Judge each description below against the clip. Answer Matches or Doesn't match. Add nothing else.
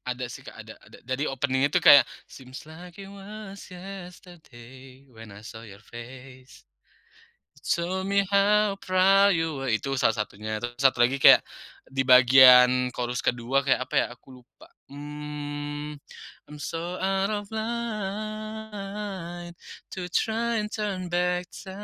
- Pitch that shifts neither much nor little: Doesn't match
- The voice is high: Doesn't match